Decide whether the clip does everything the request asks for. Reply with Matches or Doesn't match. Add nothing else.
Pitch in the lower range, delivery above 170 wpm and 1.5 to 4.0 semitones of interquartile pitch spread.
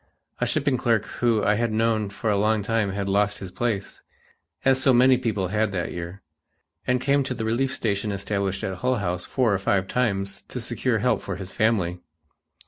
Matches